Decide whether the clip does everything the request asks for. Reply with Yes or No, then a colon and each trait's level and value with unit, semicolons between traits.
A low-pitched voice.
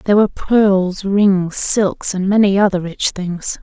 No: high, 195 Hz